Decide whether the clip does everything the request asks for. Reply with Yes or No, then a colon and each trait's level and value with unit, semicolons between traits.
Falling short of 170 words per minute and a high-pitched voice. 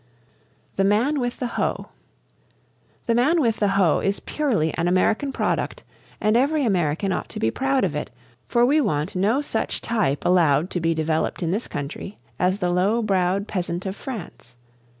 No: average, 175 wpm; high, 195 Hz